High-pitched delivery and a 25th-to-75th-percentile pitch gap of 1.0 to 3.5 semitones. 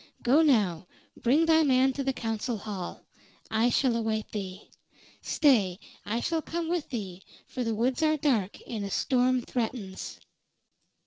No: high, 240 Hz; average, 4.6 semitones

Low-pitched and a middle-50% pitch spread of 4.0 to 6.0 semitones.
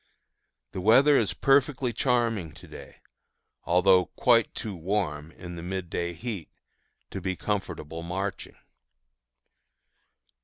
Yes: very low, 95 Hz; average, 5.0 semitones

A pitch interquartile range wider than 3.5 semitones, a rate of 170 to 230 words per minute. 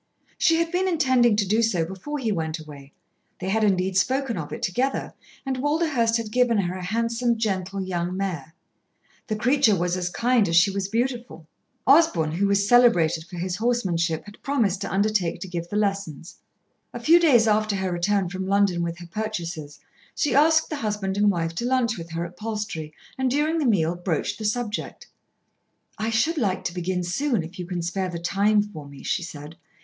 Yes: average, 5.2 semitones; average, 195 wpm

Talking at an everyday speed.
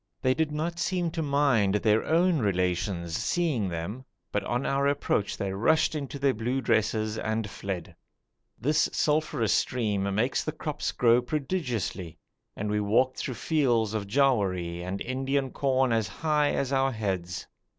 Yes: average, 155 wpm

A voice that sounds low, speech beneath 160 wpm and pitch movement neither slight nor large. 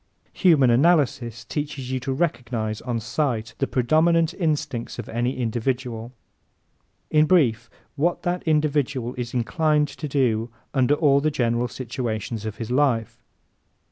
Yes: low, 130 Hz; average, 140 wpm; average, 4.2 semitones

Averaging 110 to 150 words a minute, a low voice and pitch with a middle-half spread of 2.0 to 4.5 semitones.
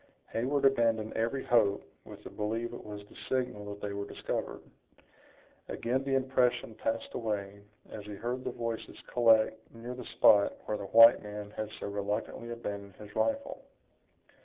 No: average, 160 wpm; low, 115 Hz; average, 2.8 semitones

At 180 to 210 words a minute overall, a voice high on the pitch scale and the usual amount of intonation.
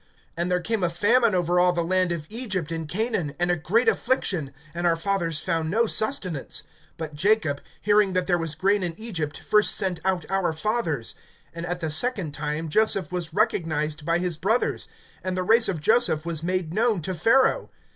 No: average, 195 wpm; medium, 180 Hz; average, 4.1 semitones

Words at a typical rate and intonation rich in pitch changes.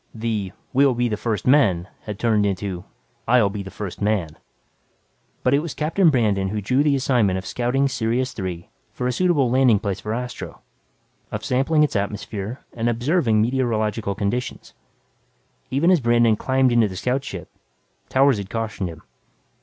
No: average, 165 wpm; average, 4.4 semitones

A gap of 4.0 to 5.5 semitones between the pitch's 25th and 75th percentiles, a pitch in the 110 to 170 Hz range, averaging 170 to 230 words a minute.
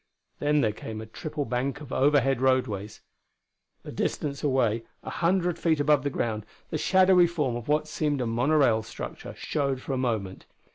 Yes: average, 4.3 semitones; low, 135 Hz; average, 180 wpm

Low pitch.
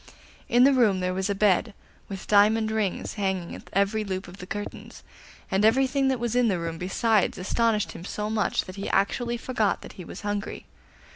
No: high, 205 Hz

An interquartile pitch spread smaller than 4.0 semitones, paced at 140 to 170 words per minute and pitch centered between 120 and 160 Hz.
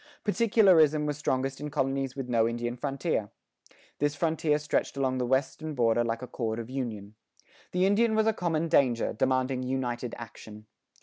No: average, 4.3 semitones; average, 165 wpm; low, 135 Hz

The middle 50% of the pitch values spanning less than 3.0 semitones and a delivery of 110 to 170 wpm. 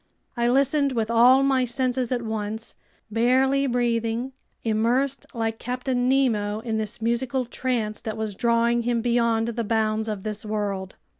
Yes: narrow, 2.4 semitones; average, 150 wpm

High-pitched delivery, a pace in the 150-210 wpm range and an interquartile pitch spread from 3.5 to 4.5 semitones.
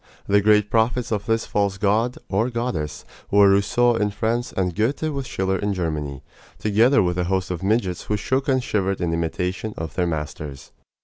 No: low, 100 Hz; average, 185 wpm; average, 4.0 semitones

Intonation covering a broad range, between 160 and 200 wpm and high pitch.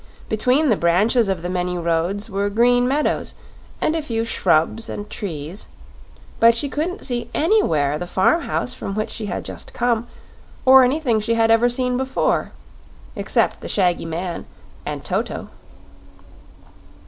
No: wide, 5.7 semitones; average, 150 wpm; high, 225 Hz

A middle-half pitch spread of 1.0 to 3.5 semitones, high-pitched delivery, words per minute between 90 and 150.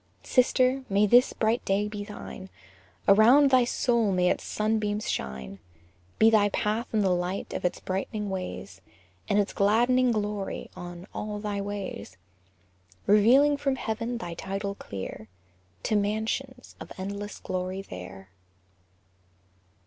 Yes: average, 3.1 semitones; high, 205 Hz; slow, 135 wpm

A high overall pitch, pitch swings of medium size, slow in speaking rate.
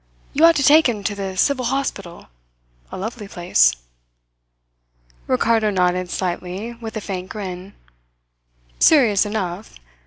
Yes: high, 205 Hz; average, 4.2 semitones; slow, 125 wpm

